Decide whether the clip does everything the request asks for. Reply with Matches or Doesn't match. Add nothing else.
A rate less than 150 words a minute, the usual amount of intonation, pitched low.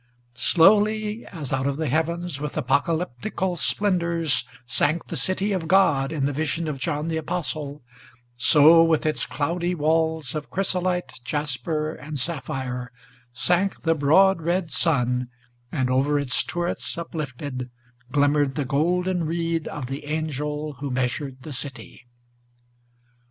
Doesn't match